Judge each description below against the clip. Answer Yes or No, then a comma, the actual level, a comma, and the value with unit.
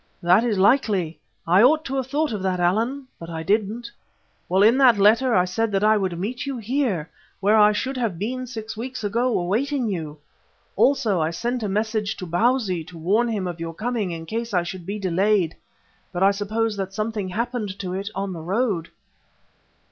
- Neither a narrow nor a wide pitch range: Yes, average, 4.3 semitones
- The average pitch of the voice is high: Yes, high, 210 Hz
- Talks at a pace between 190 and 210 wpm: Yes, average, 200 wpm